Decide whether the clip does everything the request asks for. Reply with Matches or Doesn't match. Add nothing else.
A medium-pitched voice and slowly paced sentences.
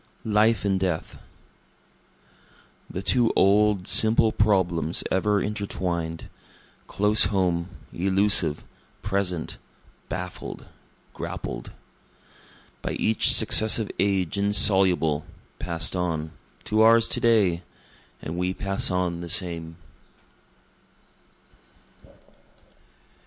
Doesn't match